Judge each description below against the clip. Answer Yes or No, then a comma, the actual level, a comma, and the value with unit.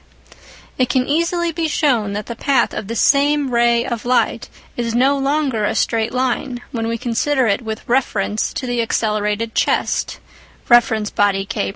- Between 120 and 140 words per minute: No, average, 170 wpm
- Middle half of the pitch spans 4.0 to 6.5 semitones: No, average, 3.6 semitones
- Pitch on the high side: Yes, high, 240 Hz